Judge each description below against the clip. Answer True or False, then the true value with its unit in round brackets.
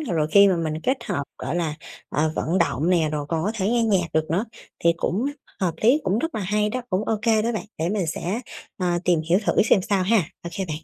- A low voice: False (185 Hz)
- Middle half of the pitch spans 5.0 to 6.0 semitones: False (4.4 semitones)